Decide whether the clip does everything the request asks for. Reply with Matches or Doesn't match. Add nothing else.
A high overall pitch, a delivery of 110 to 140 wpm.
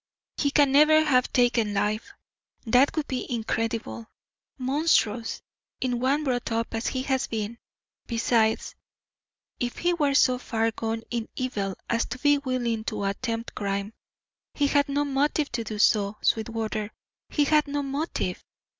Doesn't match